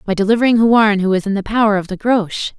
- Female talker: Yes, female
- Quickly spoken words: Yes, fast, 255 wpm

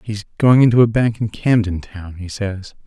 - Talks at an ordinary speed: No, fast, 210 wpm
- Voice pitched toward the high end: No, low, 105 Hz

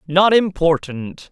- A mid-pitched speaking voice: Yes, medium, 170 Hz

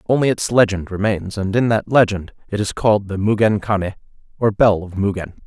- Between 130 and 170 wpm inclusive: No, average, 200 wpm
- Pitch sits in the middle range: No, low, 105 Hz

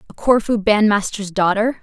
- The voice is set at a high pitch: Yes, high, 210 Hz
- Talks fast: No, slow, 130 wpm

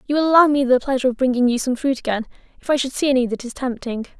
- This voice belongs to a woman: Yes, female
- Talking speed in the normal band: No, fast, 285 wpm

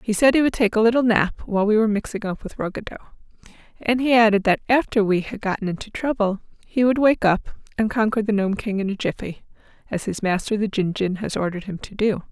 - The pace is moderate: No, fast, 230 wpm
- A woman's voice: Yes, female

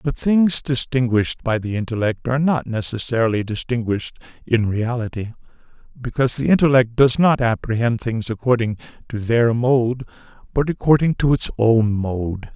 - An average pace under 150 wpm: Yes, average, 140 wpm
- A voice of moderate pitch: No, low, 120 Hz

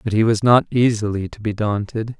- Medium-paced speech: No, fast, 220 wpm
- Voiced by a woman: No, male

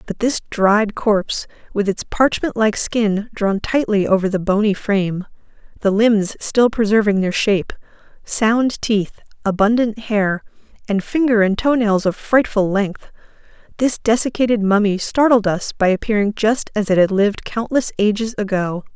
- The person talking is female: Yes, female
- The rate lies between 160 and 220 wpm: No, average, 150 wpm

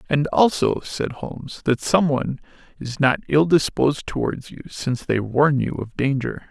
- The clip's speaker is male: Yes, male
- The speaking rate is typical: Yes, average, 165 wpm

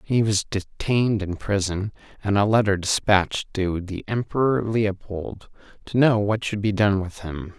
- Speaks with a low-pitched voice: Yes, low, 100 Hz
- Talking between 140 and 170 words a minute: Yes, average, 165 wpm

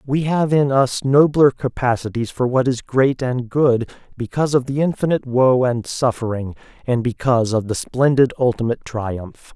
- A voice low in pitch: Yes, low, 125 Hz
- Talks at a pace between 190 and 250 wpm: No, average, 165 wpm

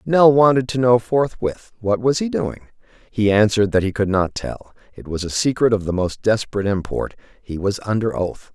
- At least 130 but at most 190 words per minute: No, fast, 205 wpm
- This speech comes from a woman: No, male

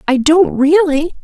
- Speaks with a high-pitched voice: Yes, very high, 310 Hz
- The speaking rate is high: No, average, 145 wpm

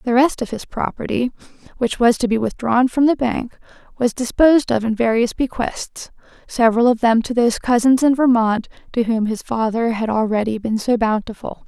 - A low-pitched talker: No, high, 235 Hz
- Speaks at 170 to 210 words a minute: Yes, average, 185 wpm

